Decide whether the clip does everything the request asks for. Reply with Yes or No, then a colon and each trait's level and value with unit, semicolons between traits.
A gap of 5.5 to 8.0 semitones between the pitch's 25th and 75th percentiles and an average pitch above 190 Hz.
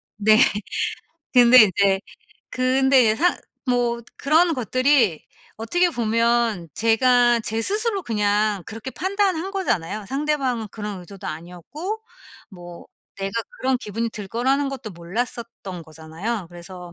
No: average, 5.1 semitones; high, 230 Hz